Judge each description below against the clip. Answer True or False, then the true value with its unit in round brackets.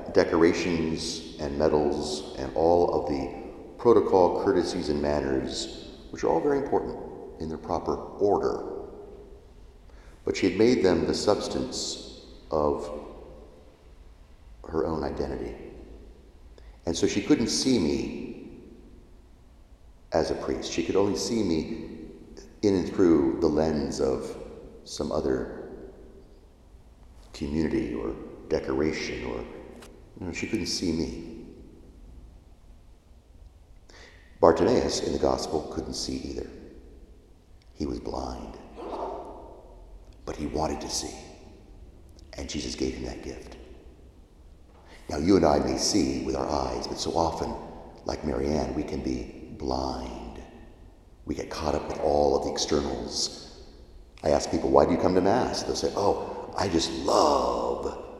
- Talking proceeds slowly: True (130 wpm)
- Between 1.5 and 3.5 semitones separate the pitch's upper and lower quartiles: True (2.8 semitones)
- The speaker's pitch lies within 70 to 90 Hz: True (80 Hz)